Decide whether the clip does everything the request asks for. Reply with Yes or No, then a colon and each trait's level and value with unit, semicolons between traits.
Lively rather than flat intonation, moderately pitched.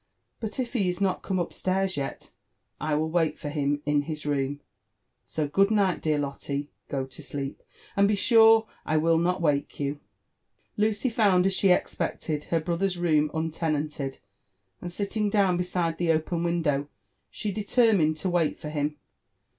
No: average, 4.5 semitones; medium, 165 Hz